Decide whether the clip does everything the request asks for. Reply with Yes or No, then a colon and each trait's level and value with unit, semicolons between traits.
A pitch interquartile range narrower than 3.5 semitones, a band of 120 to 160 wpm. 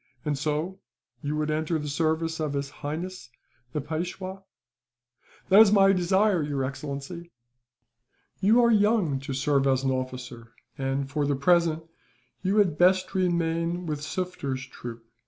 No: average, 4.7 semitones; average, 145 wpm